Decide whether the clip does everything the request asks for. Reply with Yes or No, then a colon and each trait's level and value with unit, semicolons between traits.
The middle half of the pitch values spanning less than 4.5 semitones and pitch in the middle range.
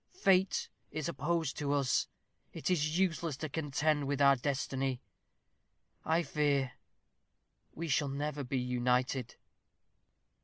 Yes: average, 2.9 semitones; medium, 145 Hz